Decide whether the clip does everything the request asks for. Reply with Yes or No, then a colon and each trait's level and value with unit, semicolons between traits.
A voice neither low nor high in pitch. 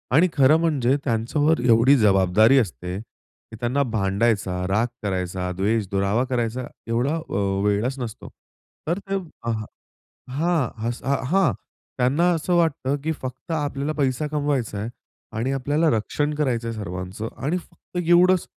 No: low, 125 Hz